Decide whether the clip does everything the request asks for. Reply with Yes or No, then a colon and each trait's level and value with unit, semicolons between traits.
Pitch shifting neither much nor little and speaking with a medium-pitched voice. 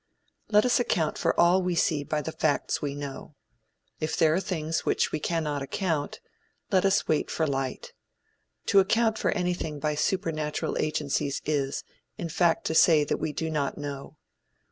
Yes: average, 3.2 semitones; medium, 155 Hz